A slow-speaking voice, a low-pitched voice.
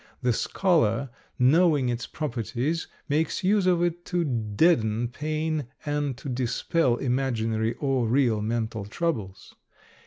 Yes: slow, 120 wpm; low, 130 Hz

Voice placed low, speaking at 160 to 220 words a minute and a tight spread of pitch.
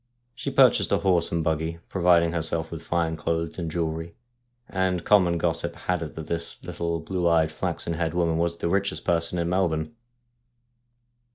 Yes: very low, 85 Hz; average, 170 wpm; narrow, 1.2 semitones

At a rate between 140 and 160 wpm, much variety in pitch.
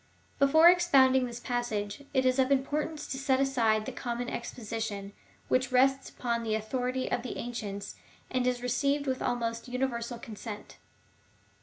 No: average, 155 wpm; narrow, 2.5 semitones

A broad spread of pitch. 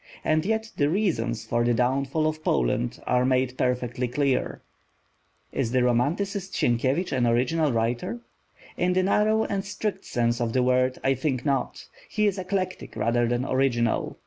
Yes: wide, 6.6 semitones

